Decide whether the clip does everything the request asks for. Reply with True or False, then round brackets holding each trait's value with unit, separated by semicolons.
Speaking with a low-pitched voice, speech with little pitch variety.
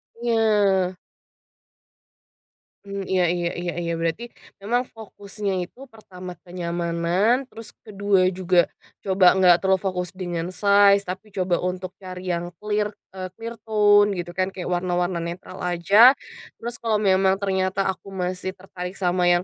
False (190 Hz; 2.3 semitones)